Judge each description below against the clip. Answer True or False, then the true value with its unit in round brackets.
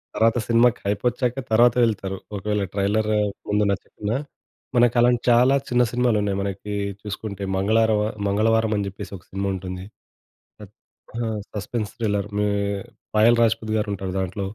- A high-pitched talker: False (105 Hz)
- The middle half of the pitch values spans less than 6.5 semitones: True (2.7 semitones)